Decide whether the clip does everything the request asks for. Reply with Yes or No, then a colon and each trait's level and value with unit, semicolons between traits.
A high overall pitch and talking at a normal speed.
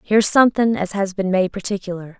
Yes: high, 195 Hz; average, 190 wpm